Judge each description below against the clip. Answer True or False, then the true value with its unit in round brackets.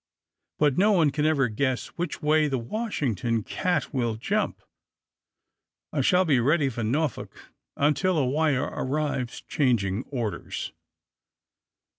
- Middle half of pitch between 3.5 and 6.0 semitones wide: True (4.4 semitones)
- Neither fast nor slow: False (125 wpm)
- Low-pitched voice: False (145 Hz)